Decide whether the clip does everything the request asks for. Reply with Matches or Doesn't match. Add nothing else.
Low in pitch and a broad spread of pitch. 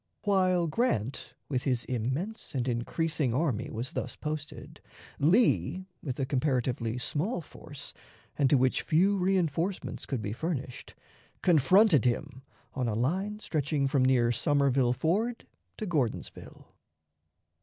Doesn't match